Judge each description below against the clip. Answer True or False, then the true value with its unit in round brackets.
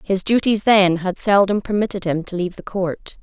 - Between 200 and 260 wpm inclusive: True (205 wpm)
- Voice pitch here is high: True (195 Hz)